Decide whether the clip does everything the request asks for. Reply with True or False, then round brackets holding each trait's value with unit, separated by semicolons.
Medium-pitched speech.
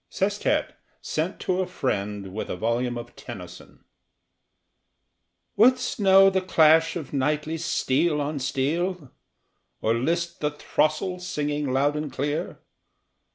True (150 Hz)